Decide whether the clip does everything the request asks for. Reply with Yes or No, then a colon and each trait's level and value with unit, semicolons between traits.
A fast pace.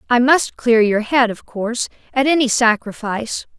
No: average, 165 wpm